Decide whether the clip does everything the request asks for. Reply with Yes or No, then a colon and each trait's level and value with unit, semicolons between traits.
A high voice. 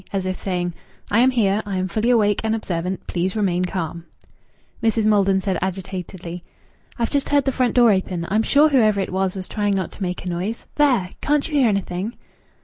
Yes: high, 195 Hz